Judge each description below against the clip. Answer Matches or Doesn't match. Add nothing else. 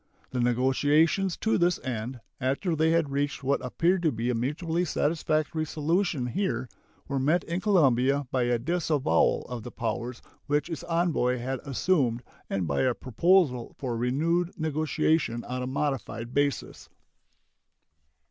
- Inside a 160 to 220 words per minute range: Doesn't match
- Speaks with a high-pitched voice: Doesn't match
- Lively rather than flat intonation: Doesn't match